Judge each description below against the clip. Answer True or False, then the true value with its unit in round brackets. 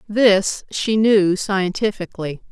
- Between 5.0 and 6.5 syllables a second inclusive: False (3.6 syllables/s)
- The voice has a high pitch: True (200 Hz)